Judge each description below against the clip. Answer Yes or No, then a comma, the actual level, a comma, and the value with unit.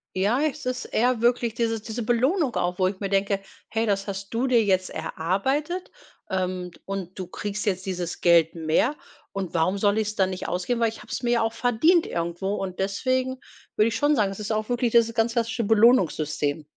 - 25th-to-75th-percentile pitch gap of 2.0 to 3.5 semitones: No, average, 4.1 semitones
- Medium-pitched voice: No, high, 210 Hz